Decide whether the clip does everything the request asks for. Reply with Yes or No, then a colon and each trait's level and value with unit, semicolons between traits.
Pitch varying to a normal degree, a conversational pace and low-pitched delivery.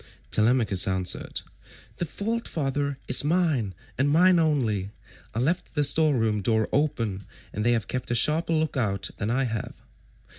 No: wide, 6.1 semitones; average, 160 wpm; low, 130 Hz